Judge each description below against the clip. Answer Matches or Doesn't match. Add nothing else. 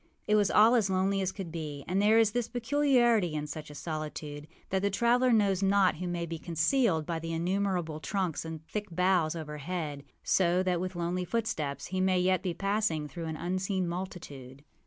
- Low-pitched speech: Doesn't match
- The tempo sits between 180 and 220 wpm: Matches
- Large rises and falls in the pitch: Doesn't match